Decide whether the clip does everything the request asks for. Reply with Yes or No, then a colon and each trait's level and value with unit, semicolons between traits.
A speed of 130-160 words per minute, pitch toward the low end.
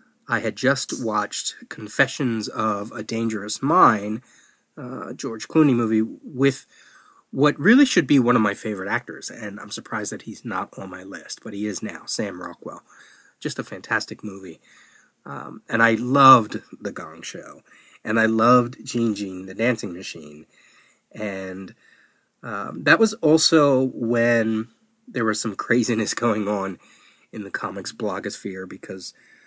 Yes: average, 155 wpm; low, 115 Hz